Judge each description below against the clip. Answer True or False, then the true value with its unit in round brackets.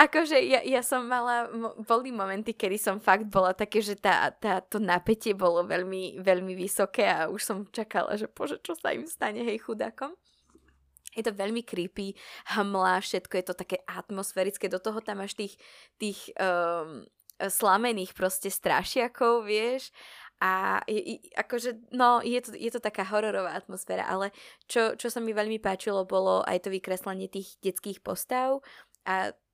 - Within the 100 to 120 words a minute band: False (165 wpm)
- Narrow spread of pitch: False (3.4 semitones)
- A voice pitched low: False (205 Hz)